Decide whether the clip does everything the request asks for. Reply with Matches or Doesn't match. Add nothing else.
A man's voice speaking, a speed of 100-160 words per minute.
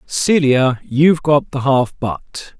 Matches